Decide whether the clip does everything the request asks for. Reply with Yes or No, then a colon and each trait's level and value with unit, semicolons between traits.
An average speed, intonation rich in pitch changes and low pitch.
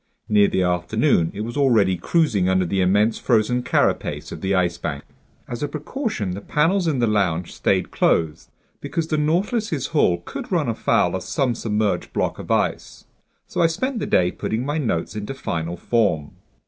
Yes: average, 180 wpm; wide, 8.3 semitones; low, 110 Hz